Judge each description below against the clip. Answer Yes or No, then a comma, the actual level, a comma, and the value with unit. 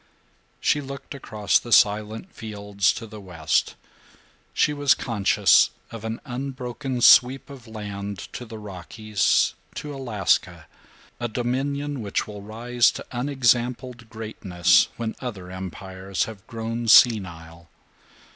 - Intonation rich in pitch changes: No, average, 3.6 semitones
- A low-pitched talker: Yes, low, 110 Hz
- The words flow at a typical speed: No, slow, 120 wpm